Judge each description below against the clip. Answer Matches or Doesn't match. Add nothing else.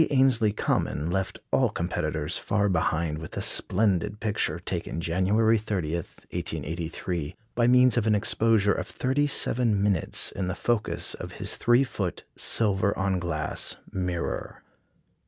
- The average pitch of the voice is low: Matches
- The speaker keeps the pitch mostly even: Doesn't match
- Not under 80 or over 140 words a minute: Matches